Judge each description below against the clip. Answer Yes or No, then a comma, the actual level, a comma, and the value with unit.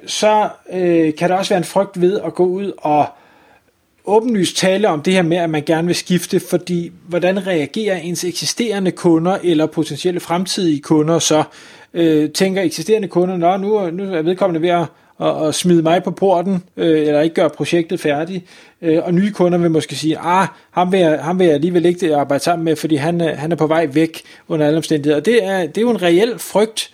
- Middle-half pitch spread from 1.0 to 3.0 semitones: Yes, average, 2.7 semitones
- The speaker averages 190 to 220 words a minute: Yes, average, 215 wpm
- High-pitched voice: No, medium, 175 Hz